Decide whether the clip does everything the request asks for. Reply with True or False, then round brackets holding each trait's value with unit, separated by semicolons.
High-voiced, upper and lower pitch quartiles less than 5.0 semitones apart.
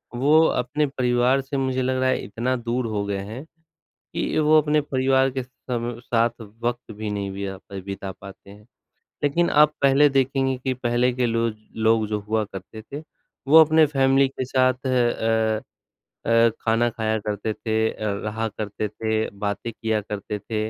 False (120 Hz; 3.3 semitones)